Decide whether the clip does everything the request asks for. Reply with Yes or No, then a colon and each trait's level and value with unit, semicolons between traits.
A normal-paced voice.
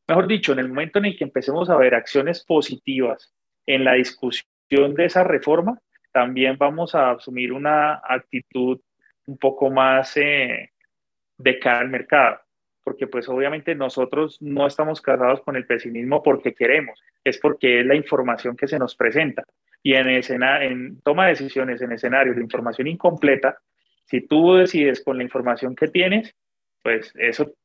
Yes: average, 165 wpm